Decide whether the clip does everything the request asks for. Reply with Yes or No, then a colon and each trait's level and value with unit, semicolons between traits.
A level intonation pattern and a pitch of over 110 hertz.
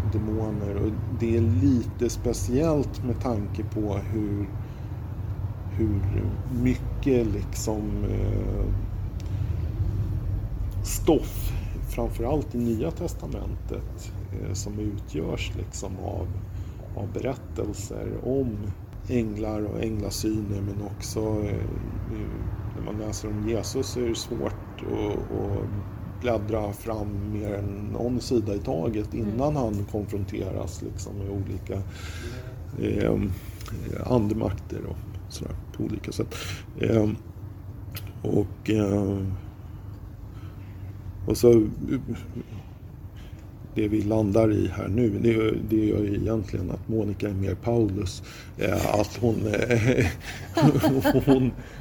No: narrow, 2.0 semitones; low, 105 Hz